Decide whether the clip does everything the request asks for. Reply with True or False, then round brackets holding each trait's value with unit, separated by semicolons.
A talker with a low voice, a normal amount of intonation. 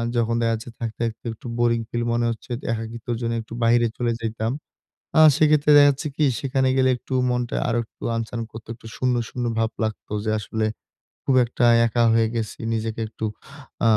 False (115 Hz; 1.5 semitones)